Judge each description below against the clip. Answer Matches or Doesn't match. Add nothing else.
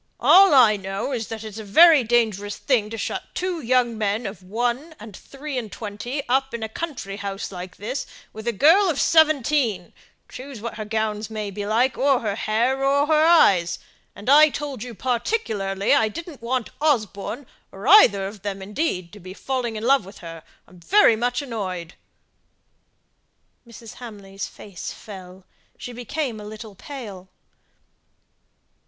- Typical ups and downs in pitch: Matches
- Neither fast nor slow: Matches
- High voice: Matches